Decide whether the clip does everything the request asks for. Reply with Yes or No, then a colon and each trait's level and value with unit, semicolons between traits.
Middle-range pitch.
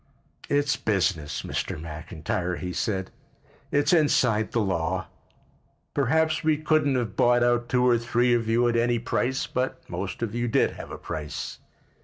No: low, 120 Hz